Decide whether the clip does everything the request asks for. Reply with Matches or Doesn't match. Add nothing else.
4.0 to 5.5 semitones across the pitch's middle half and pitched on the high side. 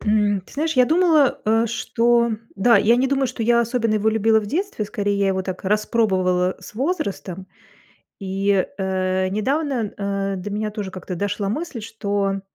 Doesn't match